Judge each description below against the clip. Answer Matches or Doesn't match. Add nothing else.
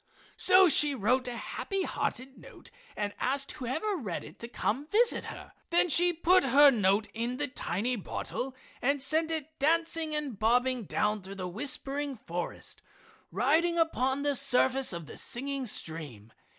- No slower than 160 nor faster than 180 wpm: Matches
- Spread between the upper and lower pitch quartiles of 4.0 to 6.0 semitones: Matches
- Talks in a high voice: Matches